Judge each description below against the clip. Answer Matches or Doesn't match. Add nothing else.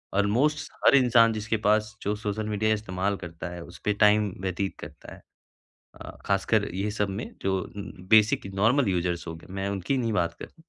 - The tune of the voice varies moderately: Doesn't match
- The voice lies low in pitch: Matches